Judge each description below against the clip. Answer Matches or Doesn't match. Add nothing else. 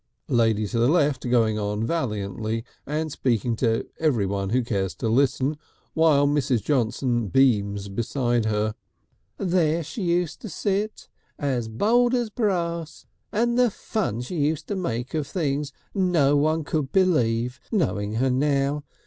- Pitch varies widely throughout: Matches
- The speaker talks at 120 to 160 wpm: Matches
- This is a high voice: Doesn't match